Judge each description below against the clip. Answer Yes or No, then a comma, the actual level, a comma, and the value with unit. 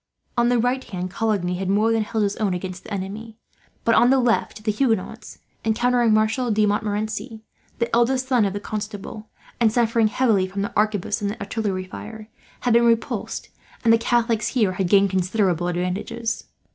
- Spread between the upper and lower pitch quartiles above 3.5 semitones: No, narrow, 2.6 semitones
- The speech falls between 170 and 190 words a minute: Yes, average, 175 wpm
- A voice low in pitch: No, high, 215 Hz